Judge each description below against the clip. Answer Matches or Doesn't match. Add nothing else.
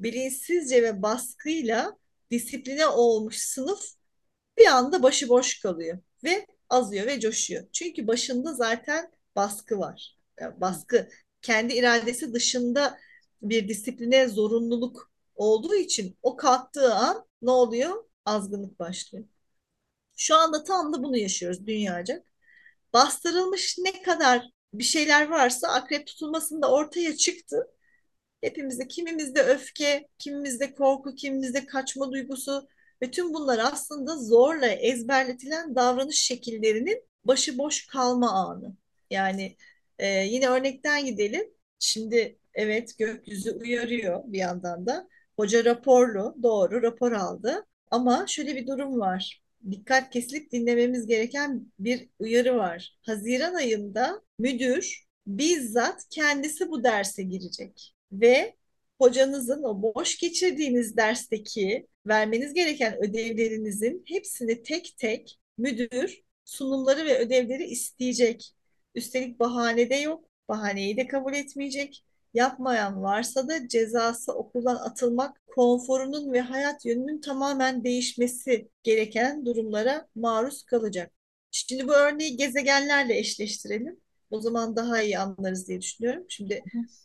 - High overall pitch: Matches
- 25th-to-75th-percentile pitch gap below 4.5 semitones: Matches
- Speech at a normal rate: Matches